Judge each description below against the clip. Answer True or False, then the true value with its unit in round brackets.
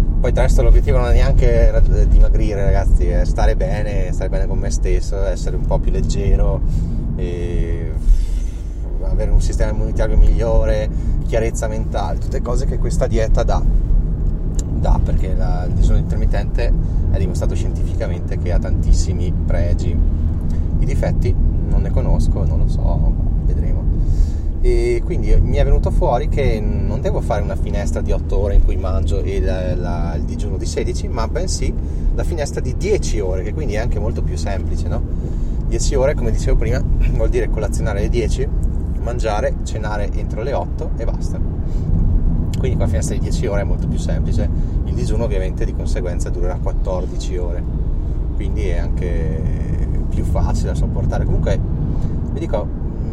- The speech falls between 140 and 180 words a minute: True (160 wpm)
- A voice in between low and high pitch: False (80 Hz)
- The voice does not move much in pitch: True (1.9 semitones)